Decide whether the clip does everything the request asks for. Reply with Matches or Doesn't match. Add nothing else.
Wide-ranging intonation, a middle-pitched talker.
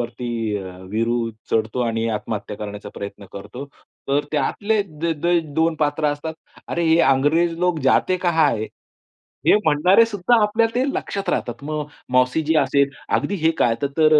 Matches